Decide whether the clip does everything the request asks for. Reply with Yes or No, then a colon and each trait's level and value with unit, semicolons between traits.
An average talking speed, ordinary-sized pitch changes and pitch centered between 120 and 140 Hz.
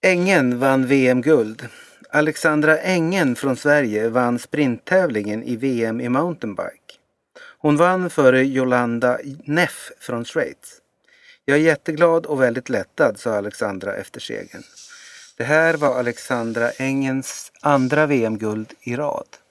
No: slow, 120 wpm; average, 4.1 semitones; low, 135 Hz